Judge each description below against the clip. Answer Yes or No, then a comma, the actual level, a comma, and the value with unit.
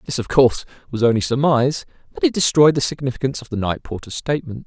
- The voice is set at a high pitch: No, low, 135 Hz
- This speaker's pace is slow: No, fast, 205 wpm